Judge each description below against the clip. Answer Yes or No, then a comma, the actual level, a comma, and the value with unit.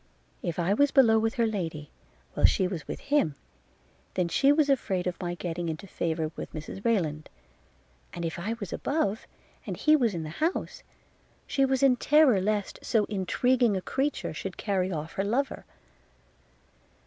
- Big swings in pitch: Yes, wide, 6.9 semitones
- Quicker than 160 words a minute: Yes, average, 170 wpm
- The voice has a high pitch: Yes, high, 200 Hz